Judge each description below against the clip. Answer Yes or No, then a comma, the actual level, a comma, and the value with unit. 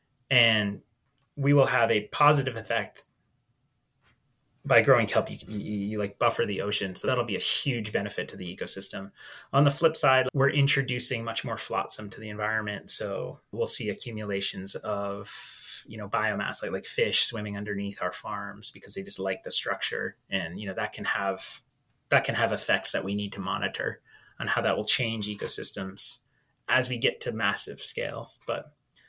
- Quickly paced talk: No, average, 180 wpm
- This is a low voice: Yes, low, 115 Hz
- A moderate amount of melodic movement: Yes, average, 4.5 semitones